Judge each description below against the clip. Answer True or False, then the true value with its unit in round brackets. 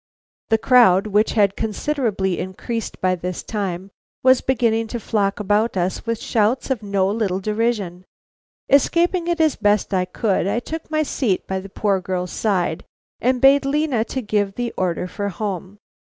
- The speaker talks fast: False (165 wpm)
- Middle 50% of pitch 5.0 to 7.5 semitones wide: False (4.2 semitones)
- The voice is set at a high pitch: True (210 Hz)